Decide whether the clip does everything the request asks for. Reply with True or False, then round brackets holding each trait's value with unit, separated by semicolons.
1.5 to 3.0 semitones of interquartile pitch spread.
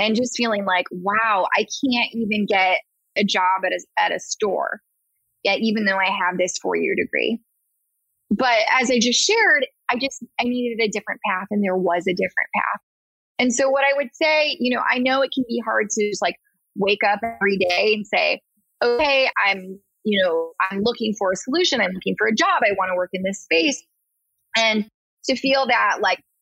False (5.0 semitones)